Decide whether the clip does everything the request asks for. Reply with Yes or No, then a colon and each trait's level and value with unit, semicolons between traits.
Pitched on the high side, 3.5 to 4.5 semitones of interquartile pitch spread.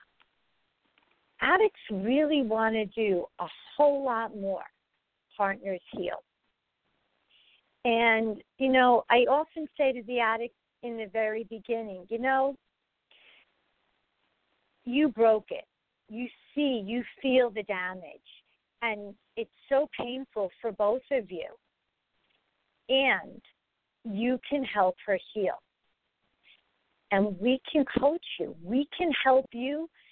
Yes: high, 235 Hz; average, 4.1 semitones